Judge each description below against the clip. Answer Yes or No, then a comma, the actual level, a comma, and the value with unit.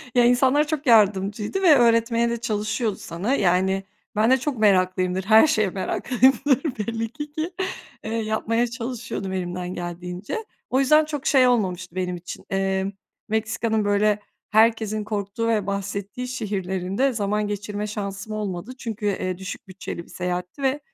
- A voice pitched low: No, high, 215 Hz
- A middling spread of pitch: Yes, average, 3.9 semitones